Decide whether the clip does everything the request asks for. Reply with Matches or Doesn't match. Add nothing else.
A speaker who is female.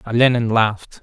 Doesn't match